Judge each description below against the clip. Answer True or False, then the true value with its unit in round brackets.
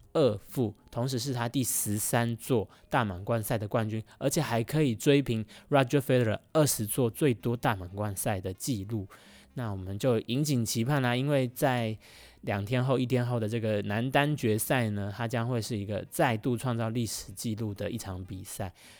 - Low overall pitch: True (115 Hz)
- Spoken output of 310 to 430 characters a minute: False (295 characters per minute)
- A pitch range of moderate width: True (3.3 semitones)